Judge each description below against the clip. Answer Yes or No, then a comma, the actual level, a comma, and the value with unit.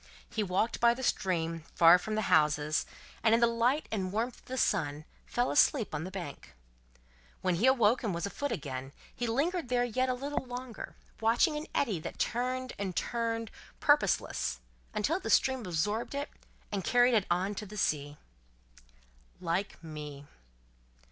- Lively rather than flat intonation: Yes, wide, 6.4 semitones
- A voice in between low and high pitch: No, high, 215 Hz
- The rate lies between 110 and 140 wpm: No, average, 170 wpm